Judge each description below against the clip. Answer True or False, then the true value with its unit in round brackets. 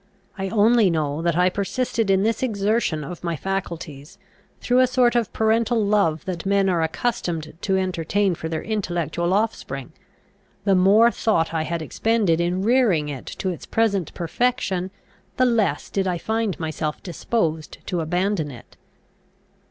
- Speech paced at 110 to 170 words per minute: True (155 wpm)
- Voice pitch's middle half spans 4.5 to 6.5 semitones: True (5.0 semitones)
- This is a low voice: False (190 Hz)